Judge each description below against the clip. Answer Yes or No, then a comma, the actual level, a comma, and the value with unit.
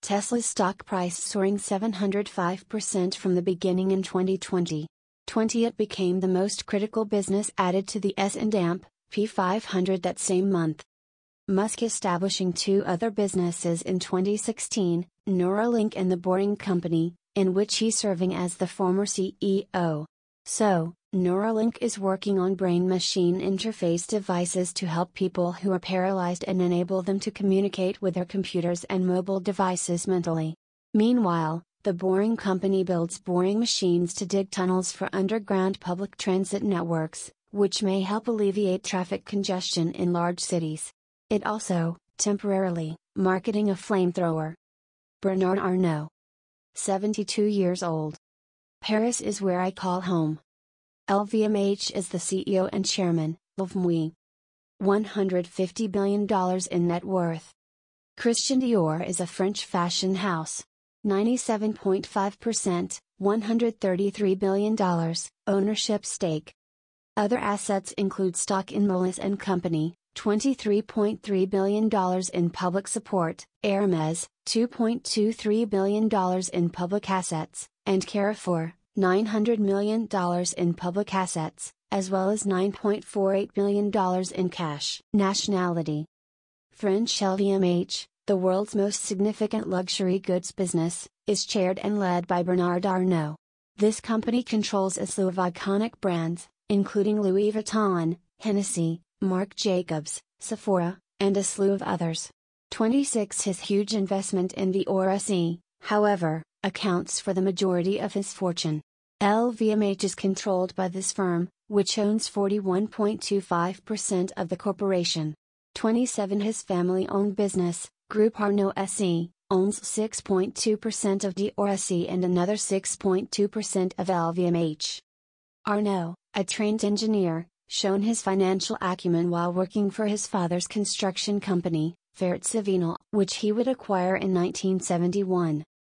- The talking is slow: Yes, slow, 125 wpm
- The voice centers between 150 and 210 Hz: Yes, high, 190 Hz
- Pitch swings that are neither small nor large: No, narrow, 2.3 semitones